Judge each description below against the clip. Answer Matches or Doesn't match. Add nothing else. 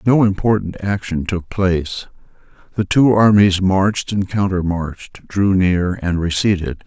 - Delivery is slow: Matches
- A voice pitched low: Matches